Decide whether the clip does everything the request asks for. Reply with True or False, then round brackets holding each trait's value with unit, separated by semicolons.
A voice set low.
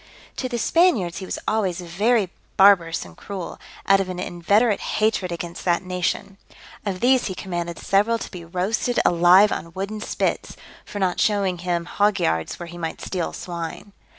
False (185 Hz)